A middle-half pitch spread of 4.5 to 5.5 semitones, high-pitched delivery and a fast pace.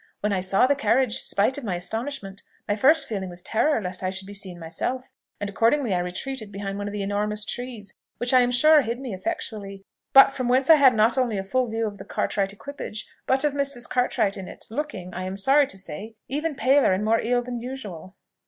Yes: average, 5.0 semitones; high, 225 Hz; fast, 225 wpm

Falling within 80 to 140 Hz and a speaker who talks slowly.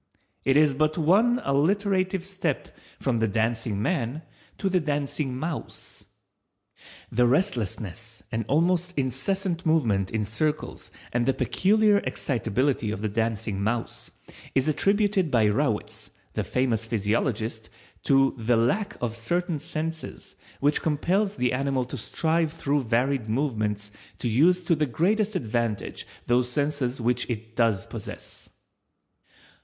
Yes: low, 135 Hz; slow, 130 wpm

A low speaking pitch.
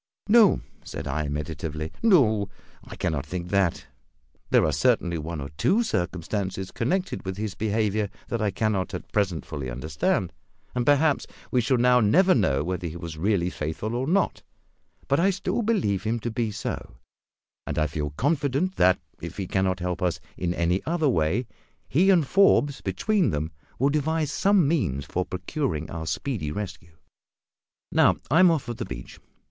Yes: low, 100 Hz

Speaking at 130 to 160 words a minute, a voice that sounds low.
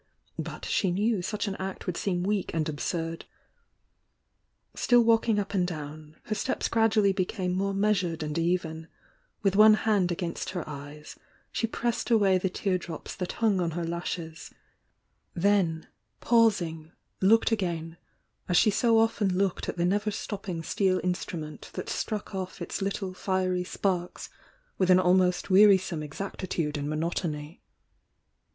No: average, 155 wpm; medium, 185 Hz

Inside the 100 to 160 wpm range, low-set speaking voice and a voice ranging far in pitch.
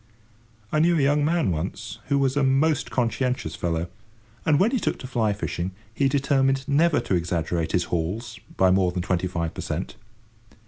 No: average, 185 wpm; low, 120 Hz; wide, 8.1 semitones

